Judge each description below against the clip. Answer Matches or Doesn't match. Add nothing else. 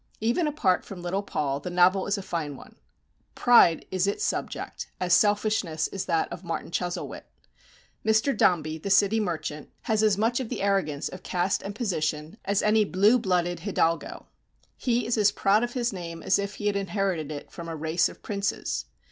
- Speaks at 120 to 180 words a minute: Doesn't match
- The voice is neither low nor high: Doesn't match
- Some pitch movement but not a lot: Matches